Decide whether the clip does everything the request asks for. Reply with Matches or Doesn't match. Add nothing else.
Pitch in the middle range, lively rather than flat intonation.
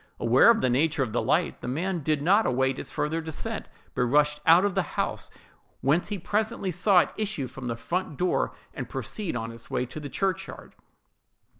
Matches